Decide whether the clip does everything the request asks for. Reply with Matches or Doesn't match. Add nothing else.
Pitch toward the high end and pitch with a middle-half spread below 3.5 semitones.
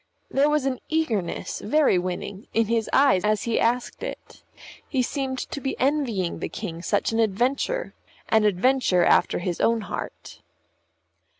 Doesn't match